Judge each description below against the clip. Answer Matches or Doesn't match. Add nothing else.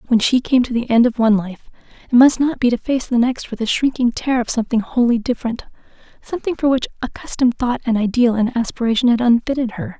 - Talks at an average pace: Doesn't match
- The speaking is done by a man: Doesn't match